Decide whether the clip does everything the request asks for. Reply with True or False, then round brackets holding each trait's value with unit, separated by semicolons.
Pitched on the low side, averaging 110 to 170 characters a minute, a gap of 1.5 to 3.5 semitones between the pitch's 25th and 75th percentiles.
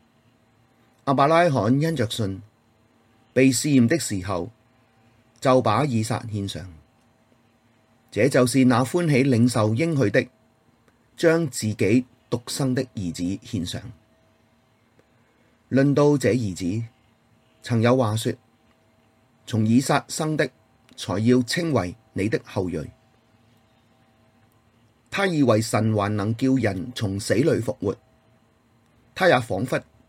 True (115 Hz; 160 characters per minute; 2.6 semitones)